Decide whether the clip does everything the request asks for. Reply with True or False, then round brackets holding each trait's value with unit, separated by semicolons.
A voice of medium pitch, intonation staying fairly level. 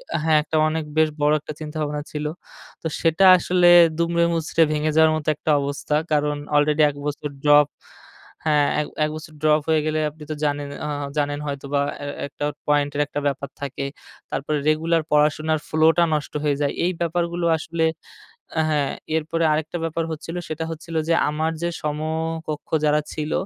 True (155 Hz; 1.5 semitones)